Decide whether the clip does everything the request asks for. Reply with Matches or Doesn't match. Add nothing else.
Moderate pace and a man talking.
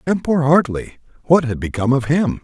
Matches